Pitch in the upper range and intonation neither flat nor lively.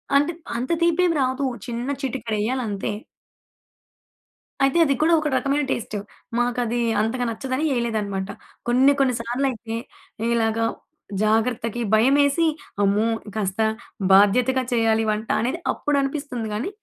Yes: high, 240 Hz; average, 3.6 semitones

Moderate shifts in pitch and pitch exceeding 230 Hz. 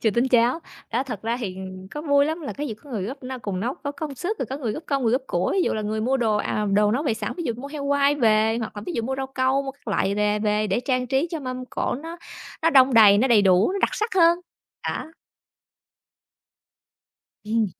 Yes: average, 4.8 semitones; very high, 255 Hz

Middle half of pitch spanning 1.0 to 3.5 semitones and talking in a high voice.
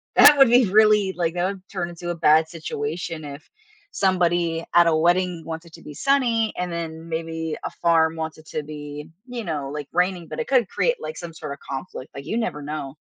No: average, 3.1 semitones; medium, 170 Hz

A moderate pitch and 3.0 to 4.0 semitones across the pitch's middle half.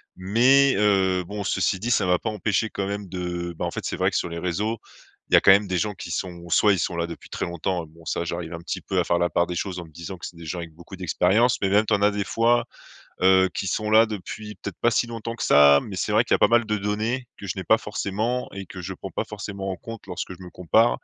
No: very low, 95 Hz; average, 3.5 semitones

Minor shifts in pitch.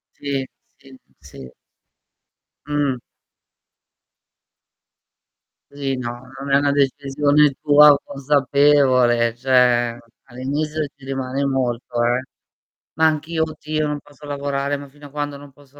Yes: narrow, 2.1 semitones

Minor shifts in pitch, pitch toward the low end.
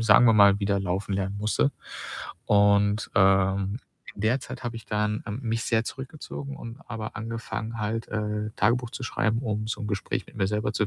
Yes: narrow, 2.1 semitones; low, 105 Hz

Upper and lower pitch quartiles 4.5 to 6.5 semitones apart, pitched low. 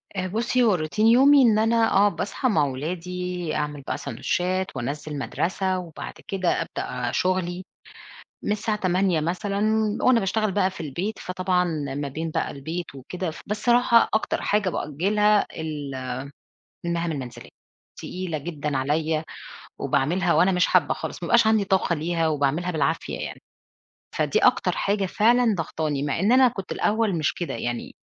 No: average, 5.1 semitones; medium, 180 Hz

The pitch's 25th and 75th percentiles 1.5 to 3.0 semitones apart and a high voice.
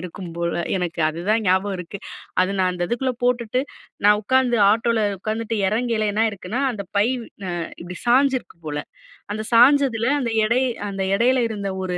No: average, 4.3 semitones; high, 215 Hz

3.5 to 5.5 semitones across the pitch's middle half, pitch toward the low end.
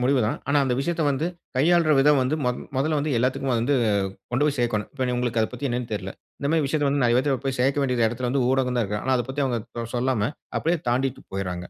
No: average, 2.8 semitones; low, 130 Hz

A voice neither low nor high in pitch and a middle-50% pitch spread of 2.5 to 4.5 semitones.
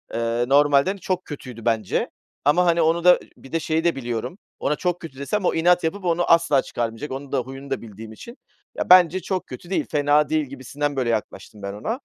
No: medium, 145 Hz; wide, 5.6 semitones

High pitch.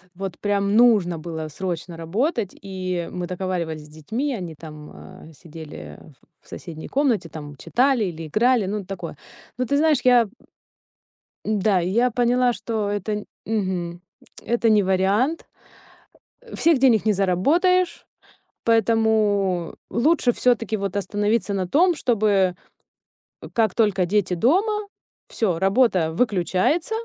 Yes: high, 205 Hz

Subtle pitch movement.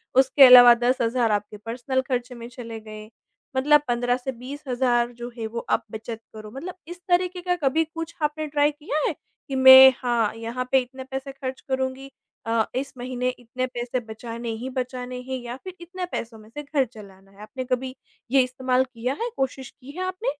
Yes: narrow, 2.3 semitones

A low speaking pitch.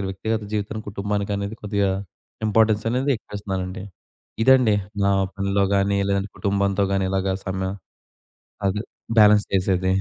Yes: low, 100 Hz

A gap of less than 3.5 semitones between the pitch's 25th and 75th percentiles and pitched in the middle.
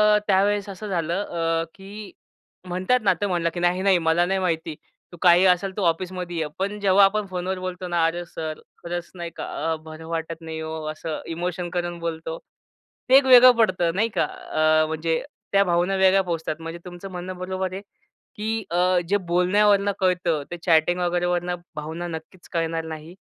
Yes: narrow, 2.5 semitones; medium, 175 Hz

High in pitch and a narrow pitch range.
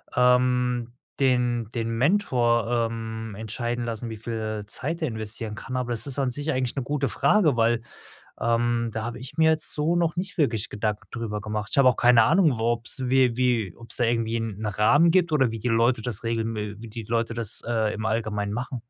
No: low, 120 Hz; narrow, 2.3 semitones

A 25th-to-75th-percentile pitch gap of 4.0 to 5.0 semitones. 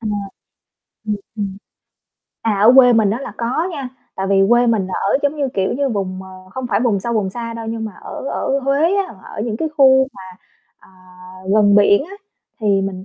Yes: average, 4.7 semitones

